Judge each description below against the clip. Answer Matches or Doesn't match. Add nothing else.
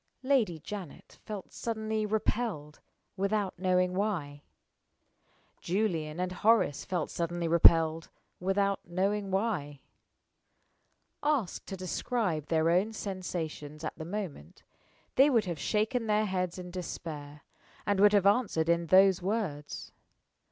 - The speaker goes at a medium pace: Doesn't match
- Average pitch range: Matches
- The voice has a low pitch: Doesn't match